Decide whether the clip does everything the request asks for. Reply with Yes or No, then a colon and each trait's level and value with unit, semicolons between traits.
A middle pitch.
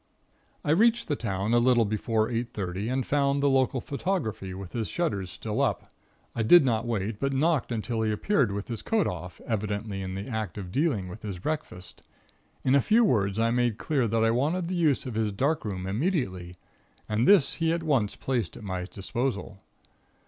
No: low, 115 Hz